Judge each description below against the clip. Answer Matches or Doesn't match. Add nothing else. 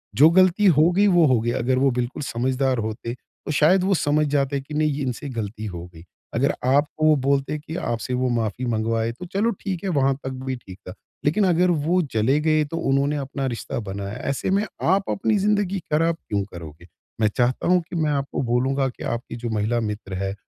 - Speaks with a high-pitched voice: Doesn't match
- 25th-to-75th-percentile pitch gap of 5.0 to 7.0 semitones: Matches